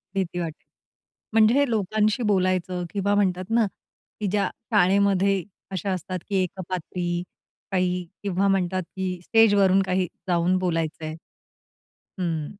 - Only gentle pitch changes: Yes, narrow, 2.0 semitones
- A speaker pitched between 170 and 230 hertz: Yes, medium, 185 Hz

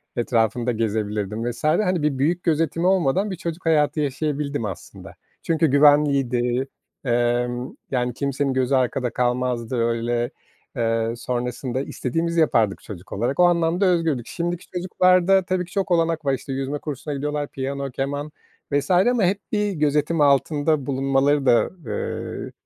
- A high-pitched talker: No, medium, 140 Hz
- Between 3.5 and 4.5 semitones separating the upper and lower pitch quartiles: No, average, 5.0 semitones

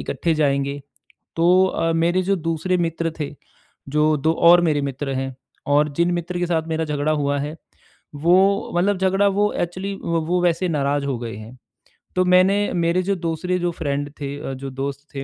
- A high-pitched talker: No, medium, 165 Hz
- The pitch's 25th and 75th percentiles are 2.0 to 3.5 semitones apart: No, average, 3.9 semitones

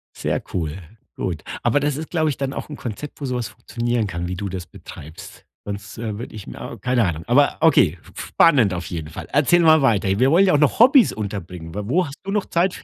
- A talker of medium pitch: No, low, 120 Hz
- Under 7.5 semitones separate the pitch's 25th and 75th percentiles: No, wide, 7.8 semitones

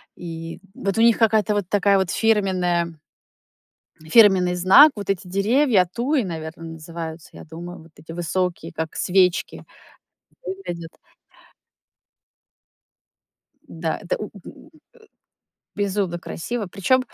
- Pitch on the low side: No, medium, 185 Hz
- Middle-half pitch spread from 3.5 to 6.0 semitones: Yes, average, 3.8 semitones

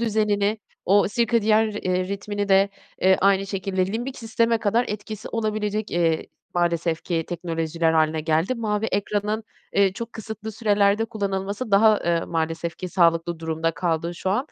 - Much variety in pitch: No, average, 4.0 semitones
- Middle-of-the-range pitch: No, high, 200 Hz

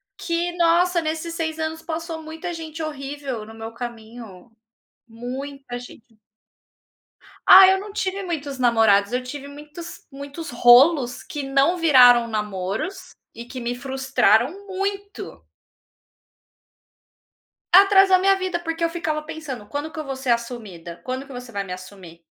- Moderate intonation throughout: No, wide, 5.8 semitones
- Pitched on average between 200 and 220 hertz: No, very high, 280 Hz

